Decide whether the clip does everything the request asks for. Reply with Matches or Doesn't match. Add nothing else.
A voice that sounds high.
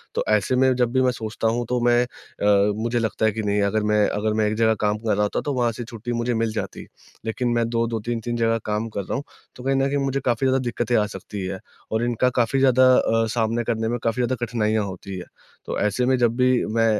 Doesn't match